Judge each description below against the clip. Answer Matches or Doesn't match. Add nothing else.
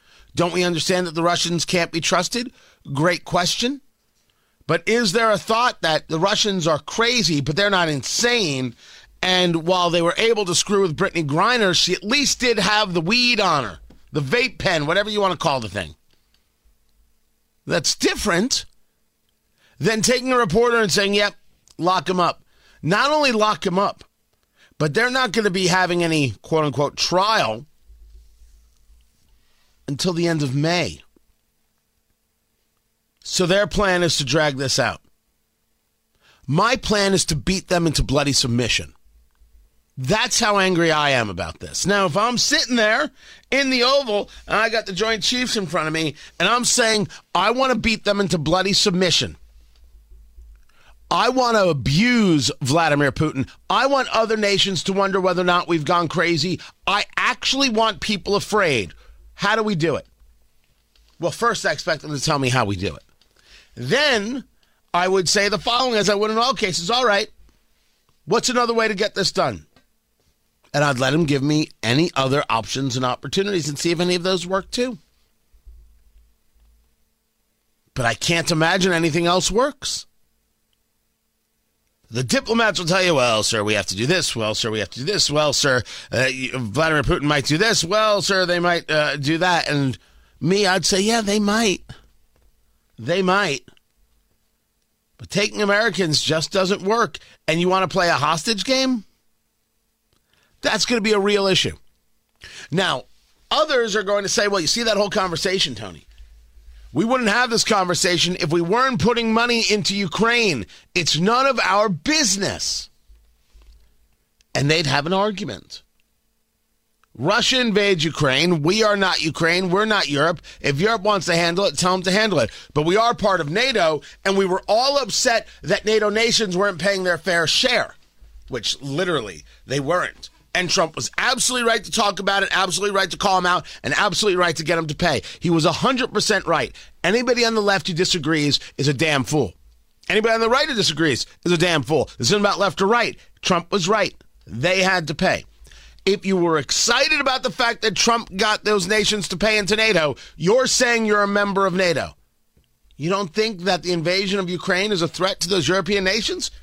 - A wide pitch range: Matches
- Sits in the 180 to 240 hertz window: Matches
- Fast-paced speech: Doesn't match